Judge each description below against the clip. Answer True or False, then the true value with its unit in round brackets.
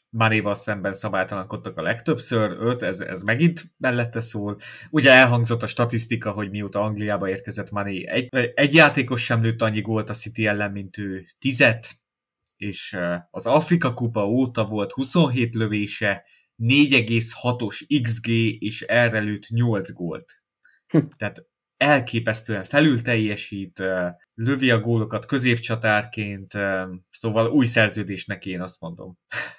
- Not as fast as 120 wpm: False (125 wpm)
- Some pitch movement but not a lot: True (3.0 semitones)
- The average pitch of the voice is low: True (110 Hz)